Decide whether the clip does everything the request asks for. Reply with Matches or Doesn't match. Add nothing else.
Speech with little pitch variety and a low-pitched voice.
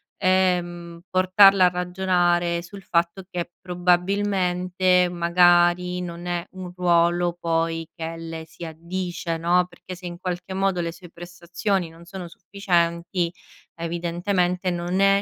Doesn't match